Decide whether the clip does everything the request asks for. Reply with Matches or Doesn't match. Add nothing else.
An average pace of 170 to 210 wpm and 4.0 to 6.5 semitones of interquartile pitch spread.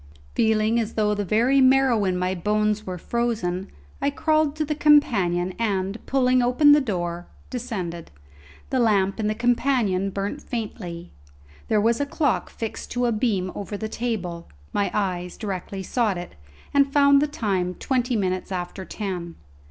Doesn't match